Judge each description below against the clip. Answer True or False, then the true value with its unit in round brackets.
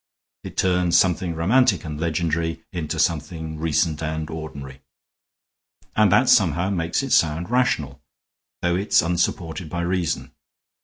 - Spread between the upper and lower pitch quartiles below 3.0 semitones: True (2.4 semitones)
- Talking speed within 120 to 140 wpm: True (135 wpm)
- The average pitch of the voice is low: True (85 Hz)